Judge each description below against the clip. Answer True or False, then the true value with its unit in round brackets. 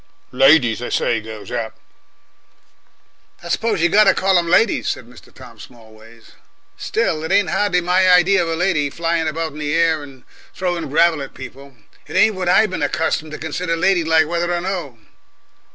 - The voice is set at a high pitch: False (165 Hz)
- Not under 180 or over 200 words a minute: True (185 wpm)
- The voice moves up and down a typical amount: True (4.5 semitones)